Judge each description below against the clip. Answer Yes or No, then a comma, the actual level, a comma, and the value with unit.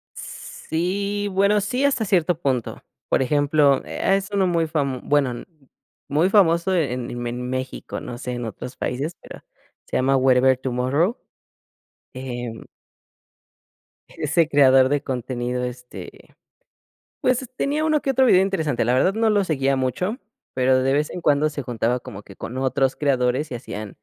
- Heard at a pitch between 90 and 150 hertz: Yes, medium, 140 Hz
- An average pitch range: No, wide, 6.2 semitones